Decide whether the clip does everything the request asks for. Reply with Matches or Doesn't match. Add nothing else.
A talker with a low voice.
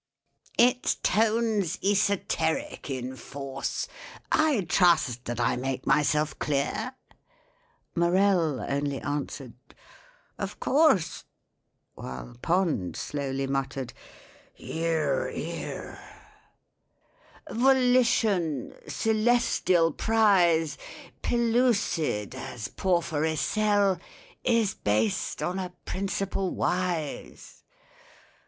Doesn't match